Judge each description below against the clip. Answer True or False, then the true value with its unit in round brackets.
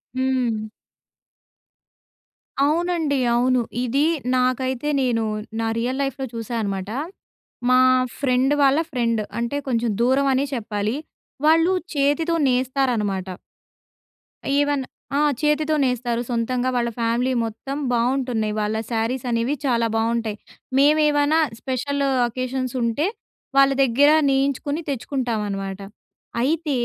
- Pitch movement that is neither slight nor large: True (3.2 semitones)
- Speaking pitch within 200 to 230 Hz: False (255 Hz)